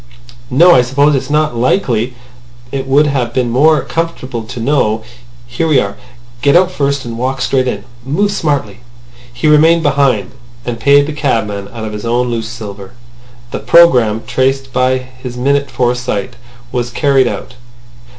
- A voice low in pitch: Yes, low, 130 Hz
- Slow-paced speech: No, average, 160 wpm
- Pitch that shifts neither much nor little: Yes, average, 3.2 semitones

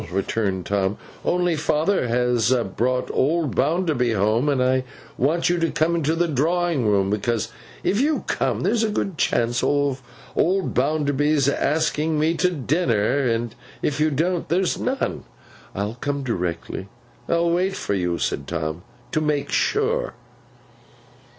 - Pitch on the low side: No, medium, 145 Hz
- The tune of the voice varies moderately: No, wide, 6.4 semitones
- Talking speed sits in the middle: Yes, average, 145 wpm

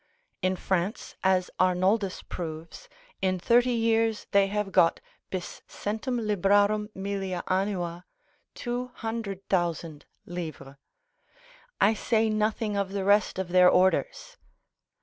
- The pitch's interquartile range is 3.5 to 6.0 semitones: No, average, 2.9 semitones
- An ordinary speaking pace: No, slow, 105 wpm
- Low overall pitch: No, high, 195 Hz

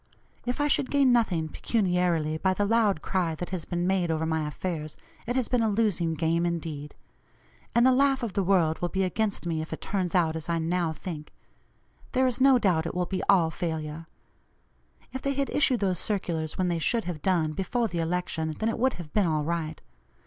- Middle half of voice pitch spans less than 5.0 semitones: No, average, 5.3 semitones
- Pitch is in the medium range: Yes, medium, 180 Hz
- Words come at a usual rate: No, fast, 215 wpm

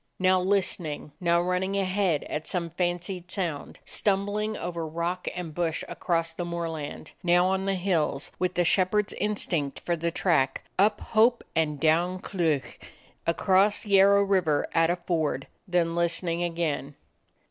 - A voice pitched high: No, medium, 175 Hz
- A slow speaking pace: No, average, 145 wpm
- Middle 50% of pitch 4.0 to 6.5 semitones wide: No, narrow, 2.5 semitones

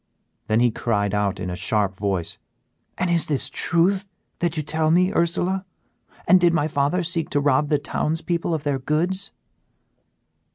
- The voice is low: No, medium, 155 Hz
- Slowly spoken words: No, average, 170 wpm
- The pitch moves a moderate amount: No, wide, 6.4 semitones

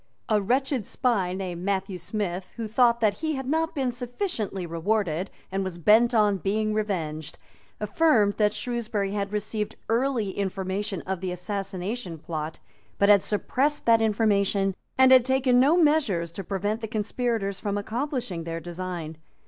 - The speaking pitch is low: No, high, 210 Hz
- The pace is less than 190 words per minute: Yes, average, 155 wpm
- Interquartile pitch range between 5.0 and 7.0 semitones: No, average, 4.1 semitones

